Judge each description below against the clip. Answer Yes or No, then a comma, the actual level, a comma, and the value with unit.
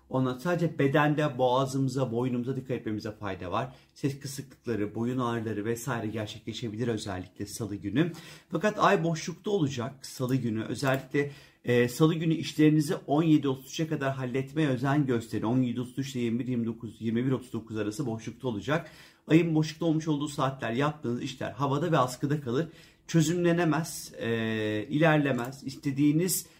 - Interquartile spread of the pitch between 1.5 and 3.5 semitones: No, average, 4.8 semitones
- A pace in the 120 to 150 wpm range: Yes, average, 125 wpm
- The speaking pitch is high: No, low, 135 Hz